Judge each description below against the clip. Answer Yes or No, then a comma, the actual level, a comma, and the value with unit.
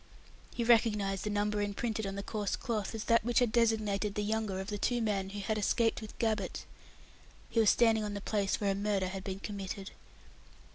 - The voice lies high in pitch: Yes, high, 210 Hz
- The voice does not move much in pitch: Yes, narrow, 2.0 semitones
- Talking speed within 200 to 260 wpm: Yes, fast, 205 wpm